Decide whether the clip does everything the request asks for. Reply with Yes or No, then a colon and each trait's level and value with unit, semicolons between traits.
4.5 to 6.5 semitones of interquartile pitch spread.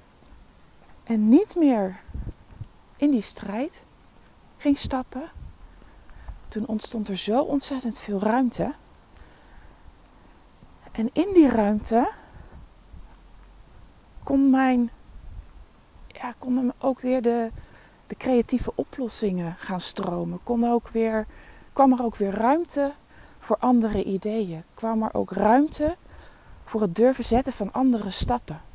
Yes: average, 4.8 semitones